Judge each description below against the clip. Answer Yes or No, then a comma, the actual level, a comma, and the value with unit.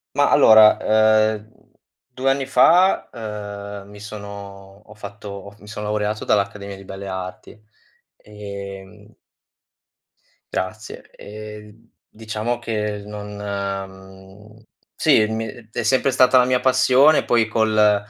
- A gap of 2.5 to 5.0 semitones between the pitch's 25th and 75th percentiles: No, narrow, 1.5 semitones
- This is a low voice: Yes, low, 105 Hz